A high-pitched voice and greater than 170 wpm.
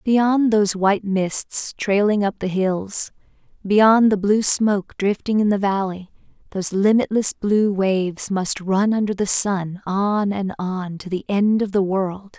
No: high, 200 Hz; average, 165 wpm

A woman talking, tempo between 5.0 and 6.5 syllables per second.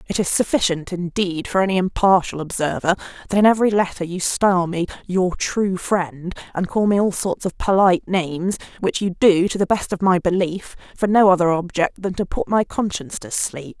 Yes: female; 5.3 syllables/s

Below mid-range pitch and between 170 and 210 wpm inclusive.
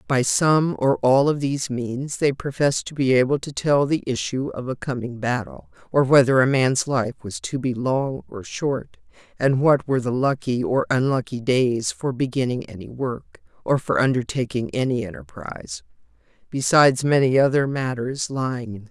Yes: low, 130 Hz; average, 180 wpm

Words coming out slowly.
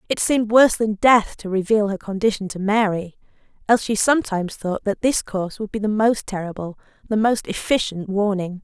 No: average, 190 wpm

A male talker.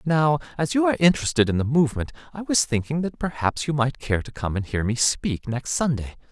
Yes: male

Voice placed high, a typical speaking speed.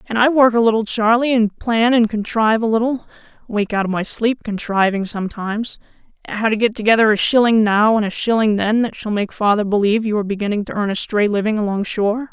No: high, 215 Hz; fast, 220 wpm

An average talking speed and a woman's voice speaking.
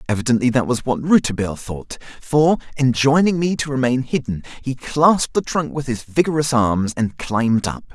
No: average, 175 wpm; male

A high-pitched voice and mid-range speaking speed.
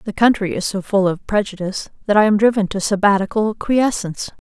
Yes: high, 205 Hz; average, 190 wpm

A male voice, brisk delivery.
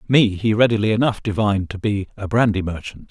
No: male; average, 195 wpm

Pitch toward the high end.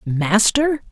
Yes: high, 205 Hz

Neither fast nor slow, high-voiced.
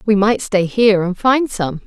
No: fast, 225 wpm; high, 210 Hz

